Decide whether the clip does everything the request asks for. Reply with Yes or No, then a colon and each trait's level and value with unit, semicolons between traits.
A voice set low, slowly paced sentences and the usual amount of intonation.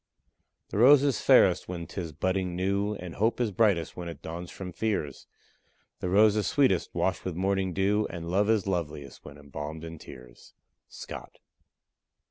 No: very low, 95 Hz; average, 165 wpm; average, 3.7 semitones